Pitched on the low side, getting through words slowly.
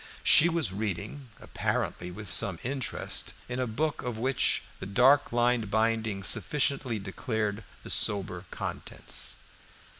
Yes: low, 110 Hz; slow, 125 wpm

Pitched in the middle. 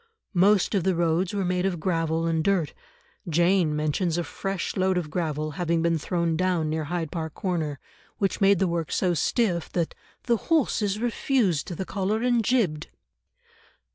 Yes: medium, 175 Hz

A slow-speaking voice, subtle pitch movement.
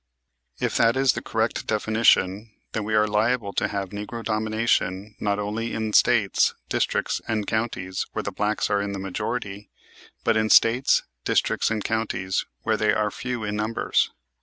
No: average, 165 wpm; narrow, 1.7 semitones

